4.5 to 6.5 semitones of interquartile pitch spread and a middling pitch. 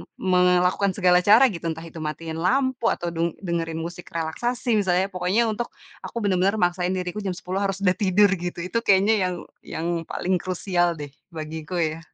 No: average, 2.8 semitones; medium, 180 Hz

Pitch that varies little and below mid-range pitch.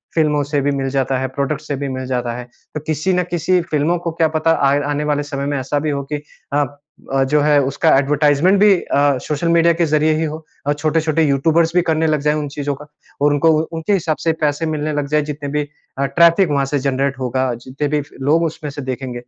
No: narrow, 2.2 semitones; medium, 150 Hz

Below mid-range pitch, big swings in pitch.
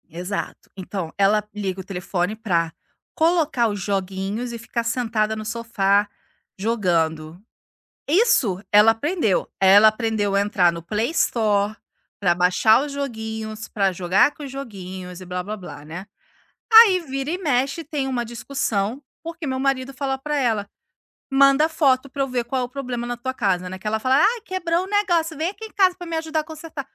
No: high, 230 Hz; wide, 6.1 semitones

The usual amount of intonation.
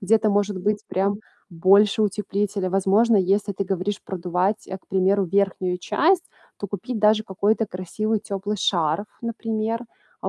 No: narrow, 2.2 semitones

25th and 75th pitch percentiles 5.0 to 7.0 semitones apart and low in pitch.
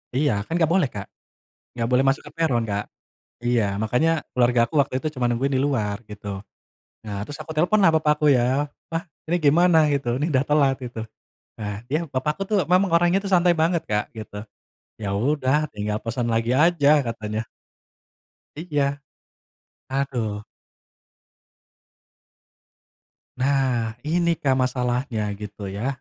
Yes: wide, 5.4 semitones; low, 130 Hz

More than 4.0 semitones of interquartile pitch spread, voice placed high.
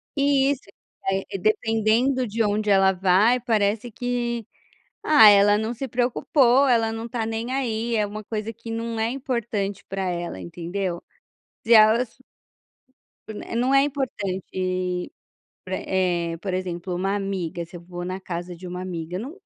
Yes: average, 4.4 semitones; high, 215 Hz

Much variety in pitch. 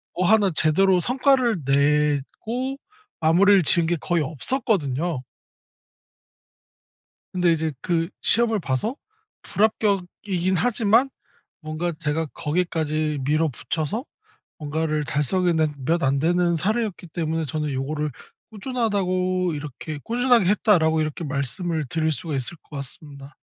No: average, 4.5 semitones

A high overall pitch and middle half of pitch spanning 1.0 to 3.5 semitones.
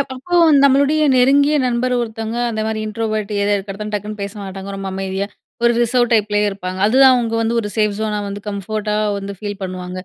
Yes: high, 215 Hz; average, 3.0 semitones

